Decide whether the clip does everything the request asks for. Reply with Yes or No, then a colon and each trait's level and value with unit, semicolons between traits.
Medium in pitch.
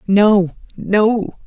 No: high, 205 Hz